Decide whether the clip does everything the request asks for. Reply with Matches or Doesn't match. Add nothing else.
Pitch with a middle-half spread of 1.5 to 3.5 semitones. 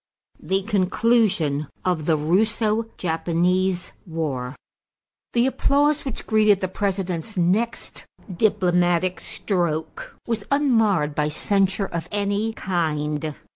Doesn't match